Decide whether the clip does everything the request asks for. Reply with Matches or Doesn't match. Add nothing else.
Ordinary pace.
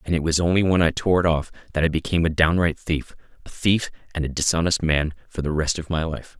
Doesn't match